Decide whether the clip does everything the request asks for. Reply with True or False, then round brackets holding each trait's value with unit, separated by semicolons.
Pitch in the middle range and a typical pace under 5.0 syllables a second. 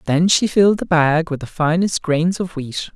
True (165 Hz; 4.7 syllables/s)